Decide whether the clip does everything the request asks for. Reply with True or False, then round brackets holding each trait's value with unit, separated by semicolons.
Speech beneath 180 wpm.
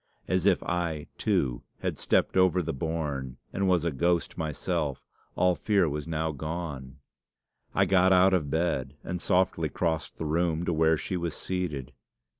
True (165 wpm)